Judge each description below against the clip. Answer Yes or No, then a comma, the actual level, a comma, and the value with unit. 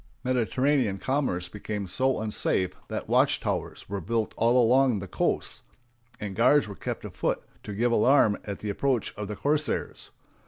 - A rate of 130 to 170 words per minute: Yes, average, 160 wpm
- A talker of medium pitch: No, low, 115 Hz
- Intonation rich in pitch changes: No, average, 4.2 semitones